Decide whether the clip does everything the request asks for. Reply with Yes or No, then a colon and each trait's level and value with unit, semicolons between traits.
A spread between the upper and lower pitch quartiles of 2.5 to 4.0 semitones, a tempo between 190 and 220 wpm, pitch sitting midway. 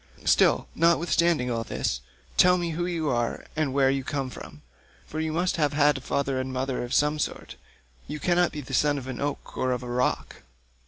Yes: average, 3.6 semitones; average, 200 wpm; medium, 145 Hz